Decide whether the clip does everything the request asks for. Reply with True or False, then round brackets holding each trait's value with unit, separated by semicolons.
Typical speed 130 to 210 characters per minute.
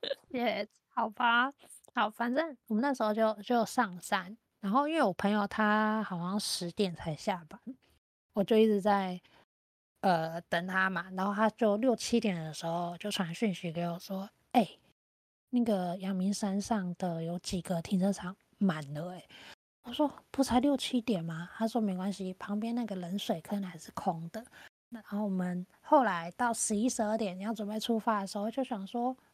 False (255 characters per minute)